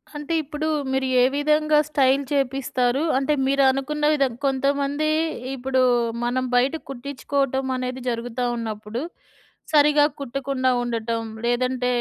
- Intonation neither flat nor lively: No, narrow, 2.2 semitones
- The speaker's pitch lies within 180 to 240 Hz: No, very high, 265 Hz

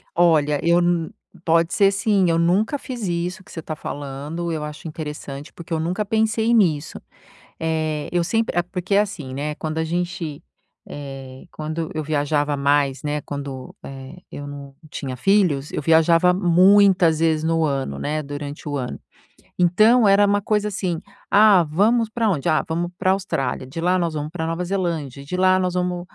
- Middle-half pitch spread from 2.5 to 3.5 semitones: No, average, 4.0 semitones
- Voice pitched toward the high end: No, medium, 165 Hz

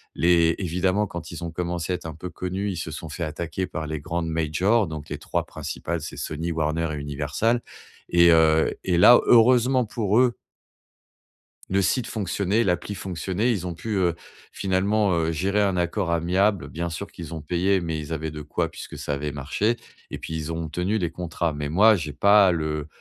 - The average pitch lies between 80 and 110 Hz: Yes, very low, 85 Hz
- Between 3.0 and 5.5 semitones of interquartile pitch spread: Yes, average, 3.6 semitones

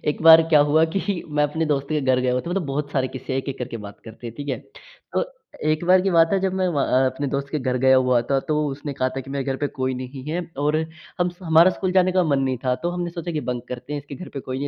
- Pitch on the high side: No, medium, 145 Hz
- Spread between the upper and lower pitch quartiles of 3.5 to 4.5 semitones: Yes, average, 4.2 semitones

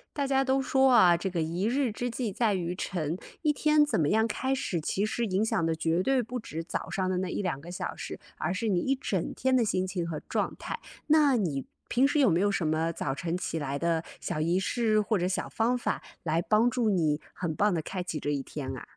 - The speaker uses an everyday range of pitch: No, wide, 6.5 semitones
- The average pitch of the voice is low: No, high, 190 Hz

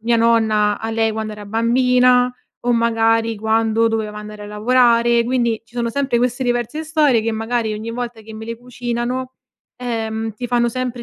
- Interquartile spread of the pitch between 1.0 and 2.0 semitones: Yes, narrow, 1.7 semitones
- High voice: Yes, high, 230 Hz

